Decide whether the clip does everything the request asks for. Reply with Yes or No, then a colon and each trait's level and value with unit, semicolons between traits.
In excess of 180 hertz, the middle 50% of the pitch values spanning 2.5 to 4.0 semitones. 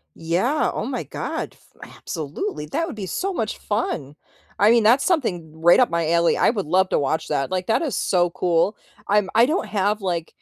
No: high, 190 Hz; average, 5.2 semitones